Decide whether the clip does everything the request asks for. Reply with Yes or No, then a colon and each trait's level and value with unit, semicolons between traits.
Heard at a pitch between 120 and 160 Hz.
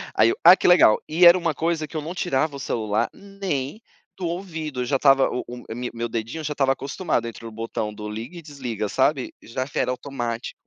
Yes: low, 135 Hz